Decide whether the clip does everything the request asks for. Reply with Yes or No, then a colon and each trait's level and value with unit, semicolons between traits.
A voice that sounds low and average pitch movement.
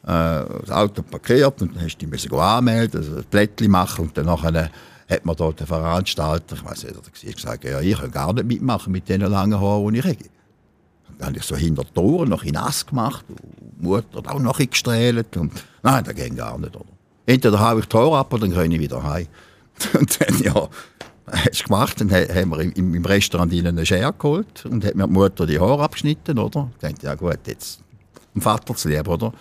No: very low, 95 Hz; wide, 5.8 semitones